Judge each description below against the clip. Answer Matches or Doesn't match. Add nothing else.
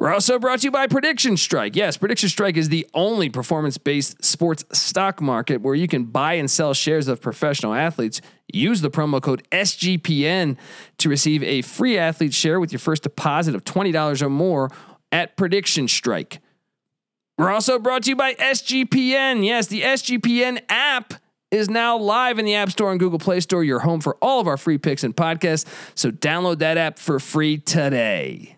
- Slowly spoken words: Doesn't match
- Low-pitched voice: Doesn't match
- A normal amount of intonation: Doesn't match